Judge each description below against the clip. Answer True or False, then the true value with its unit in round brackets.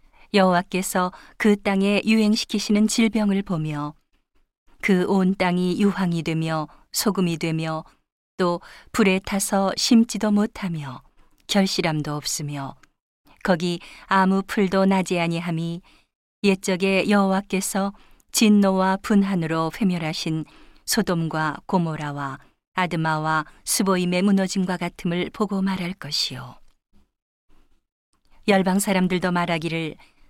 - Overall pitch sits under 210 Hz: True (185 Hz)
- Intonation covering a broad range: False (3.2 semitones)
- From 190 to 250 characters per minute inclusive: True (240 characters per minute)